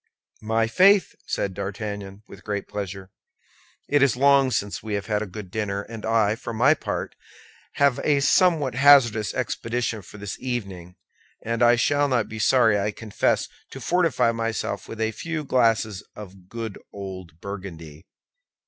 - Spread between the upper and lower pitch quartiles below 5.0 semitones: Yes, average, 4.1 semitones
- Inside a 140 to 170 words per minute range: Yes, average, 155 wpm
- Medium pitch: No, low, 110 Hz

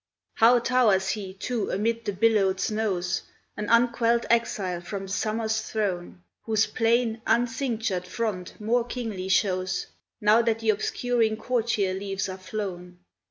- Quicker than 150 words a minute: No, slow, 135 wpm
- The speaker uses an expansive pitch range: No, average, 3.3 semitones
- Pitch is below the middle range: No, high, 215 Hz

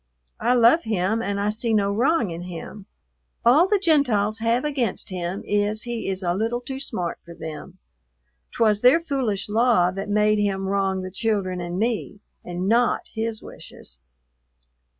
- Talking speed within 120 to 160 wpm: No, average, 170 wpm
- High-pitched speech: Yes, high, 210 Hz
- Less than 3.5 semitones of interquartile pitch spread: No, average, 3.8 semitones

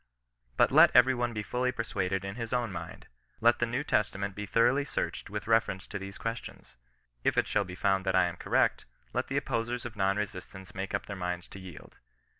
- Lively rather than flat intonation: No, average, 3.7 semitones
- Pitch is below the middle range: Yes, low, 105 Hz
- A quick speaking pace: Yes, fast, 215 wpm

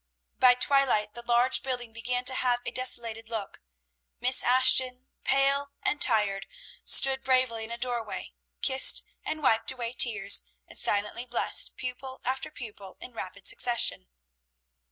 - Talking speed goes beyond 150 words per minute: No, average, 140 wpm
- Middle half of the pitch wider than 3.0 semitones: No, narrow, 2.4 semitones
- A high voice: Yes, high, 245 Hz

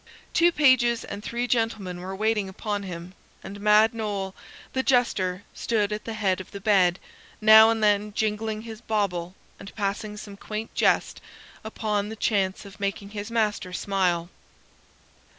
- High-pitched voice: Yes, high, 210 Hz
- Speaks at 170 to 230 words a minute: No, average, 155 wpm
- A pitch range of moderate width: No, narrow, 2.2 semitones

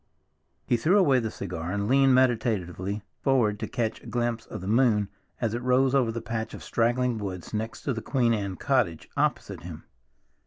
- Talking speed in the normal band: Yes, average, 190 wpm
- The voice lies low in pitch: Yes, low, 115 Hz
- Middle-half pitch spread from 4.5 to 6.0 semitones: No, average, 3.6 semitones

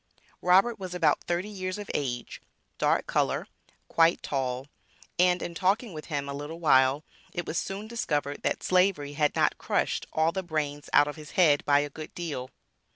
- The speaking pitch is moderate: Yes, medium, 160 Hz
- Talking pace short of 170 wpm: No, average, 180 wpm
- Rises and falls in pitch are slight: No, average, 4.1 semitones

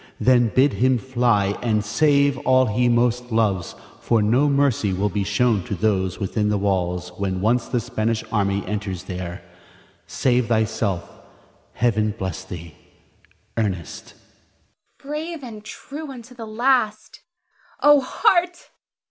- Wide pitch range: Yes, wide, 6.0 semitones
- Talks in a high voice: No, low, 115 Hz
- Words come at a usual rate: No, slow, 130 wpm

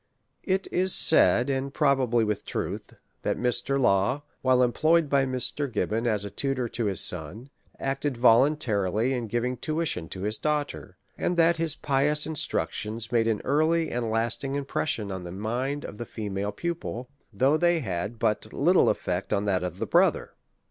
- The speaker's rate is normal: Yes, average, 165 wpm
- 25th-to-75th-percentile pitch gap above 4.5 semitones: Yes, average, 5.1 semitones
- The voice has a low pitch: Yes, low, 125 Hz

